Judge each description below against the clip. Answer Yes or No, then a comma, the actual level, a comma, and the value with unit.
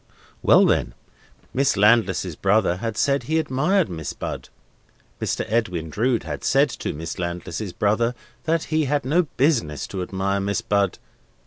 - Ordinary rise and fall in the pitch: No, wide, 7.0 semitones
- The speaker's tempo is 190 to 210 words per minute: No, average, 150 wpm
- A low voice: Yes, low, 105 Hz